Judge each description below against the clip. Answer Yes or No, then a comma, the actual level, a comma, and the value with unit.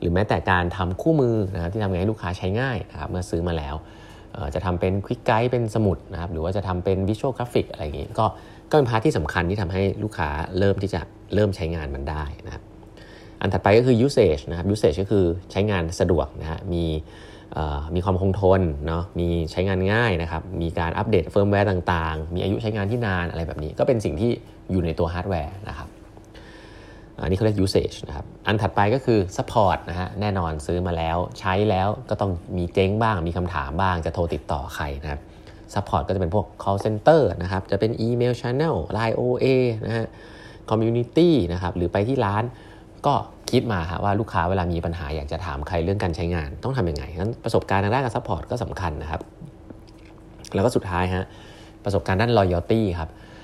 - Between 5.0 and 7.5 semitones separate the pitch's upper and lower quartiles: No, average, 4.0 semitones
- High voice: No, very low, 95 Hz